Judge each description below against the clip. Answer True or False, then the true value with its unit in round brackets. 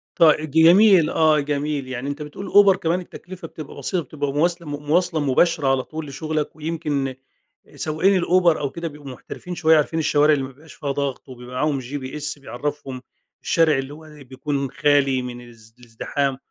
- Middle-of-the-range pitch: True (150 Hz)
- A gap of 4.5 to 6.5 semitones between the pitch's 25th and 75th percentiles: False (3.0 semitones)